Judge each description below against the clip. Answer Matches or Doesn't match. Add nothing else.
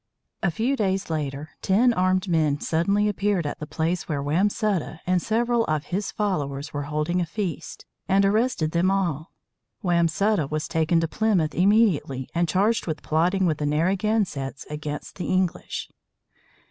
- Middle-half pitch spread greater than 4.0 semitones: Matches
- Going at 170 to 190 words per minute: Doesn't match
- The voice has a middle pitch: Matches